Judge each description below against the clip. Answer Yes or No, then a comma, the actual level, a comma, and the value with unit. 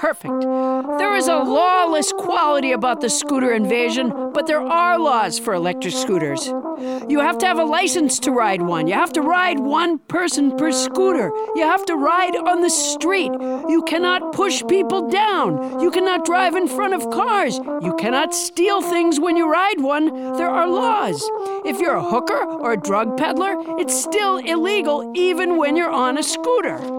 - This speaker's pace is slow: No, average, 180 wpm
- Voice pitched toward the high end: Yes, very high, 320 Hz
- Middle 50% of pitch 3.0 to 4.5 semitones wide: No, wide, 5.4 semitones